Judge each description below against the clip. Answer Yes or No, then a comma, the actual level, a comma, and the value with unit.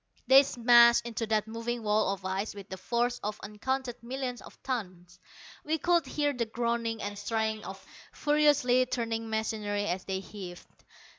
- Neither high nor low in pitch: No, high, 225 Hz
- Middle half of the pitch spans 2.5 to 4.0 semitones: Yes, average, 3.1 semitones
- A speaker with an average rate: Yes, average, 160 wpm